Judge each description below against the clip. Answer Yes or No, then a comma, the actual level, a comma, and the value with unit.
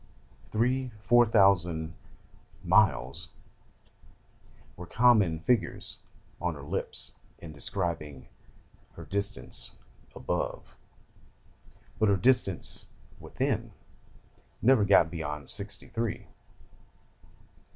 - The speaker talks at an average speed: No, slow, 80 wpm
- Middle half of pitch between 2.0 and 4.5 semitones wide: No, wide, 5.5 semitones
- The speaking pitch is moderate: No, very low, 95 Hz